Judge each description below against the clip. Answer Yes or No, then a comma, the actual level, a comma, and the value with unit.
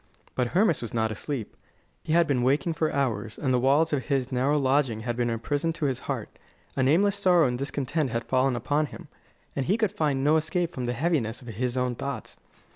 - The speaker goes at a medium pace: No, fast, 220 wpm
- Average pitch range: Yes, average, 4.1 semitones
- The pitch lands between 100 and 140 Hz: Yes, low, 135 Hz